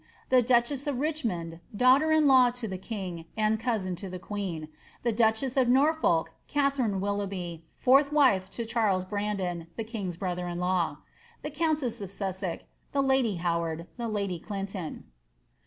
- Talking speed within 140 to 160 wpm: Yes, average, 155 wpm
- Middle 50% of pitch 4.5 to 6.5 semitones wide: Yes, wide, 5.6 semitones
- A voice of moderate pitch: No, high, 210 Hz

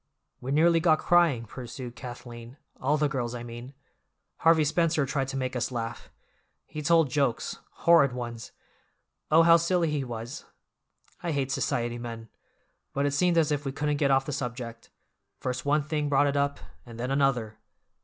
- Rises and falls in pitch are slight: No, average, 3.8 semitones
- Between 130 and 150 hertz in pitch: Yes, low, 135 Hz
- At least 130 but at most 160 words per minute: No, average, 170 wpm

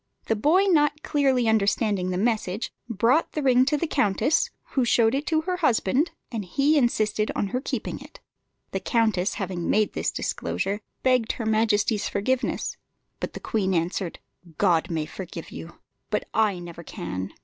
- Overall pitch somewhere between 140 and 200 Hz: No, high, 220 Hz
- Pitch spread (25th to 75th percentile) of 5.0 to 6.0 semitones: Yes, wide, 5.5 semitones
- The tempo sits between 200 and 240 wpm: No, average, 165 wpm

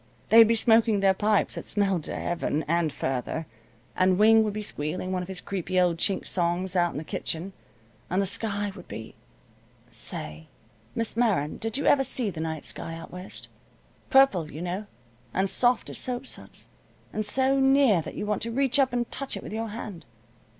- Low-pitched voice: No, high, 200 Hz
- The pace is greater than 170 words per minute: Yes, average, 195 wpm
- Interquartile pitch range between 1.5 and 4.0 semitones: No, average, 4.6 semitones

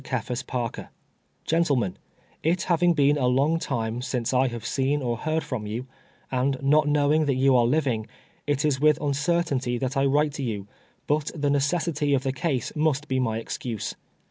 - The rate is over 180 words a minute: Yes, average, 190 wpm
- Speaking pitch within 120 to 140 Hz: Yes, low, 135 Hz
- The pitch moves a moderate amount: Yes, average, 3.2 semitones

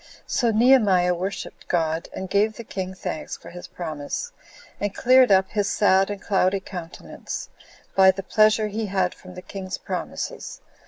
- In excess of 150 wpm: Yes, average, 160 wpm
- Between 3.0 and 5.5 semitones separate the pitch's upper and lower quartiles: No, narrow, 2.6 semitones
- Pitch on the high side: Yes, high, 195 Hz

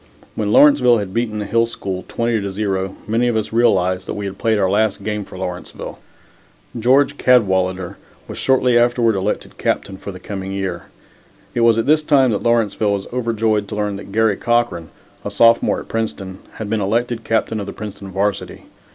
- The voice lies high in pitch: No, low, 105 Hz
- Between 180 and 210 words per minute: Yes, average, 190 wpm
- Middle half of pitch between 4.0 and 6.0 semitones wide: No, average, 3.2 semitones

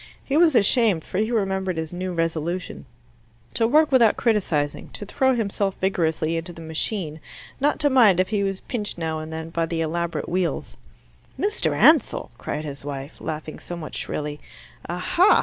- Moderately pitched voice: Yes, medium, 180 Hz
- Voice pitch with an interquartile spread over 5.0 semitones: Yes, wide, 5.4 semitones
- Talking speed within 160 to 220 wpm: Yes, average, 165 wpm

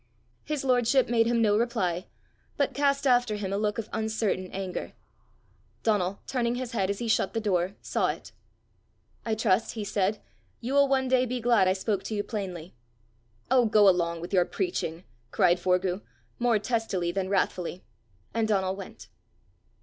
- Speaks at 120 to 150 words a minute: No, average, 170 wpm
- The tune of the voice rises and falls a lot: No, average, 4.2 semitones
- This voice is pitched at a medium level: No, high, 210 Hz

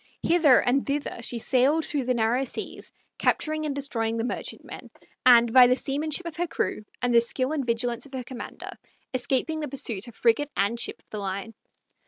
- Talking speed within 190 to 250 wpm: Yes, average, 195 wpm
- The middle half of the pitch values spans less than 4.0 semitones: Yes, average, 3.6 semitones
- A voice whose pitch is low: No, very high, 255 Hz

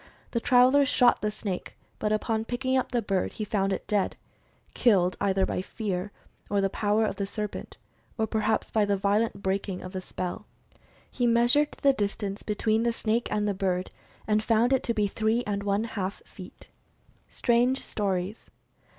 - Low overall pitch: No, high, 210 Hz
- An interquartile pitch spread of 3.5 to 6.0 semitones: No, average, 2.9 semitones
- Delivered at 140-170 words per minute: No, average, 180 wpm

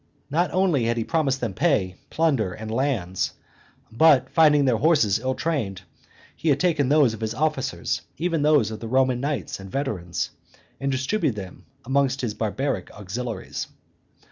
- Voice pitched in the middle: No, low, 130 Hz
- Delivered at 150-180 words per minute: Yes, average, 160 wpm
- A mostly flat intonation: No, average, 5.1 semitones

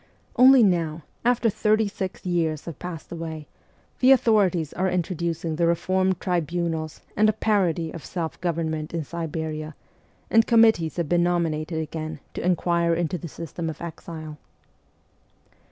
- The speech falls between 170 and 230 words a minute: No, average, 140 wpm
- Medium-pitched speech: Yes, medium, 170 Hz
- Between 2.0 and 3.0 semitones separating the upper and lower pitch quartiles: Yes, average, 2.7 semitones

